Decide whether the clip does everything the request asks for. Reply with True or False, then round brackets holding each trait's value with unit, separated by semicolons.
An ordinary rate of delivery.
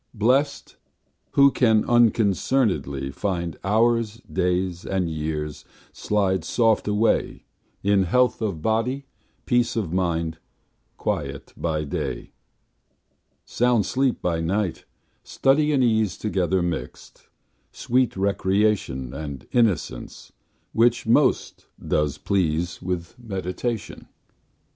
False (100 wpm)